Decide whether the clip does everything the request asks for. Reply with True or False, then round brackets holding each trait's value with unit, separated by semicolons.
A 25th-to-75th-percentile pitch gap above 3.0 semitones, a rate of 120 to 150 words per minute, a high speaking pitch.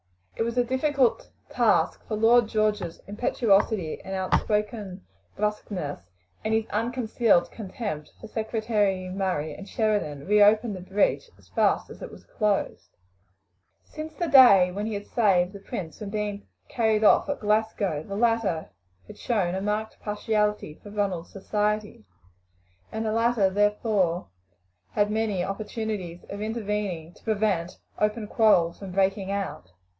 False (2.5 semitones; 140 wpm; 210 Hz)